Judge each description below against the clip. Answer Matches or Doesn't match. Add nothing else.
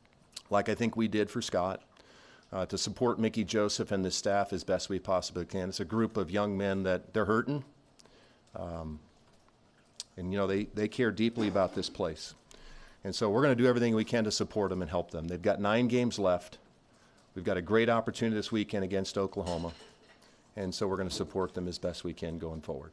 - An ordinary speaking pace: Doesn't match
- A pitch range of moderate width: Matches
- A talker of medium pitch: Doesn't match